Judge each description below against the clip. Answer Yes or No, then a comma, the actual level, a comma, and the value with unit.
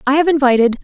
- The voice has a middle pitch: No, very high, 275 Hz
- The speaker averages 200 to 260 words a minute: Yes, fast, 215 wpm